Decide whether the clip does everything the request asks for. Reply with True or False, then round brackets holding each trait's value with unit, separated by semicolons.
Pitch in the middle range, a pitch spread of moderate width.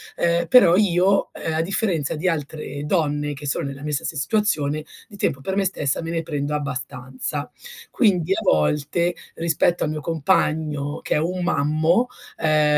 True (155 Hz; 3.1 semitones)